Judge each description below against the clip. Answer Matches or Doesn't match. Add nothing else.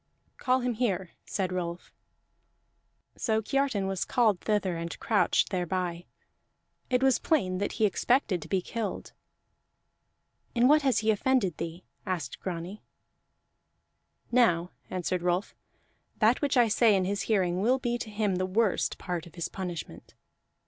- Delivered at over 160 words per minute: Doesn't match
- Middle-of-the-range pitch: Doesn't match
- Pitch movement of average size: Matches